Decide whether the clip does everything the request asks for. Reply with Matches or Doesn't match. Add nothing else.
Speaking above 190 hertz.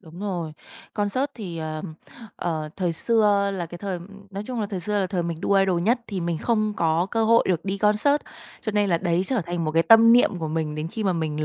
Doesn't match